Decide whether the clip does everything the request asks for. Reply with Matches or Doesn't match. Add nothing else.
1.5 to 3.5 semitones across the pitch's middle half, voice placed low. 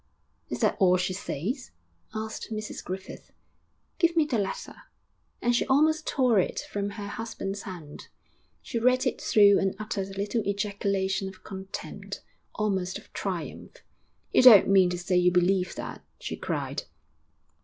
Doesn't match